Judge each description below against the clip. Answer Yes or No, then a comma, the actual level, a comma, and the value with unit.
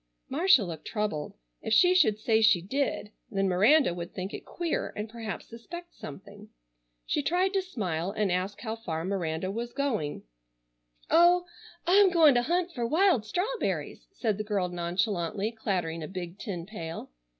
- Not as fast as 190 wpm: Yes, average, 160 wpm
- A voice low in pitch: No, high, 215 Hz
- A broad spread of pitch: Yes, wide, 8.3 semitones